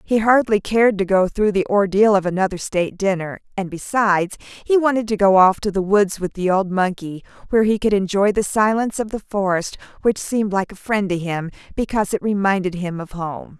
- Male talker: No, female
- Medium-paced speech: No, fast, 210 wpm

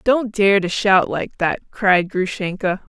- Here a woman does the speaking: Yes, female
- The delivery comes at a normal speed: Yes, average, 165 wpm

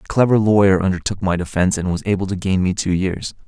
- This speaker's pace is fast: Yes, fast, 240 wpm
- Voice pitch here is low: Yes, very low, 95 Hz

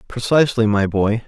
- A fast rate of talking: No, average, 140 wpm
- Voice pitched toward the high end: No, low, 115 Hz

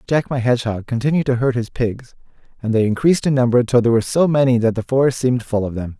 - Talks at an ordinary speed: No, fast, 250 wpm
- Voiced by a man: Yes, male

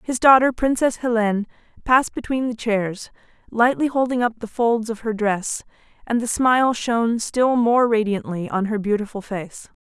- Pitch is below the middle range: No, high, 230 Hz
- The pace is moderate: Yes, average, 165 wpm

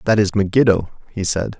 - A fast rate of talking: No, average, 190 wpm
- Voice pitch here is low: Yes, low, 105 Hz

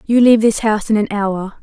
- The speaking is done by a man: No, female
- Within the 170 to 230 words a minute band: No, fast, 260 wpm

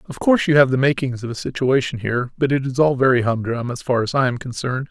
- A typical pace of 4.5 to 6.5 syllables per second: No, 6.7 syllables/s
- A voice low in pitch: Yes, low, 130 Hz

